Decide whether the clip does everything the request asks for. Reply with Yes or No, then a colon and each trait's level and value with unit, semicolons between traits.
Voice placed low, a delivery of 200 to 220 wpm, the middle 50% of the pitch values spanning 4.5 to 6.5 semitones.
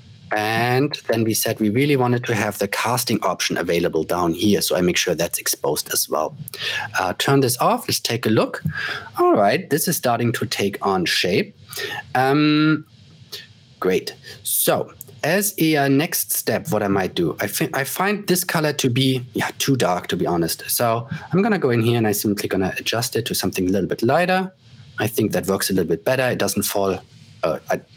Yes: low, 130 Hz; fast, 205 wpm; average, 5.2 semitones